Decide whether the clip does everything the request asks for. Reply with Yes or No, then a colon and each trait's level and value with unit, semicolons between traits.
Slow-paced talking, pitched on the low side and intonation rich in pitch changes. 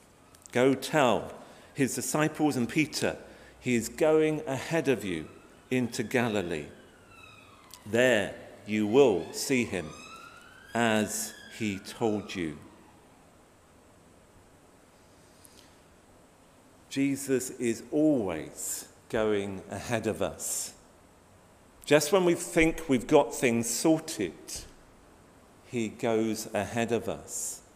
Yes: slow, 95 wpm; low, 115 Hz; wide, 6.1 semitones